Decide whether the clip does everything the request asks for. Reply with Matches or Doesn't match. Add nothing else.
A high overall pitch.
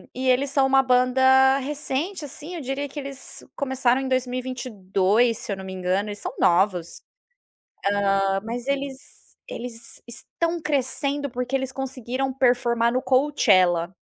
Matches